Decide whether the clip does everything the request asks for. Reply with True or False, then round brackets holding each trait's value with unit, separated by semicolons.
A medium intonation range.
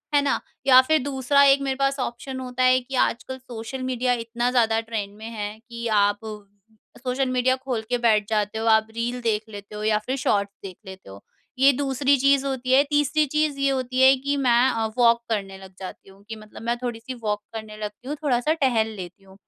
True (3.5 semitones)